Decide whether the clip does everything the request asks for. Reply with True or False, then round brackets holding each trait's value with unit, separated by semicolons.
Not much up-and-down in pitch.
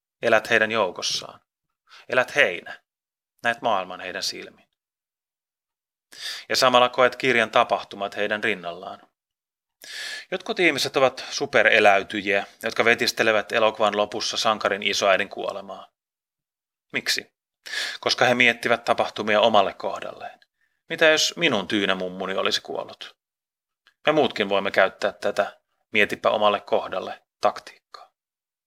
False (3.2 semitones)